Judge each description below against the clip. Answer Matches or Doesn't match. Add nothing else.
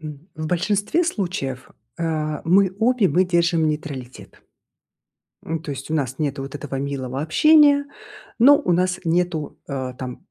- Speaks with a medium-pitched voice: Matches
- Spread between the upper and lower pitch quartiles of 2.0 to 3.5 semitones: Doesn't match